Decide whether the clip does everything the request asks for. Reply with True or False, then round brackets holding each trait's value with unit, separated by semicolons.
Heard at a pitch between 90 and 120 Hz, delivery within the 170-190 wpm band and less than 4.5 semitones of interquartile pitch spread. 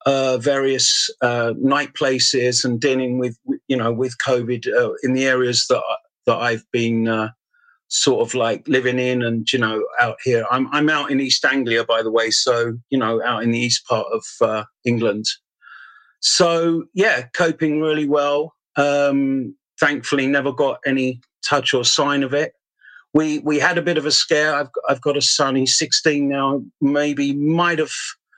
False (135 Hz; 180 wpm; 3.7 semitones)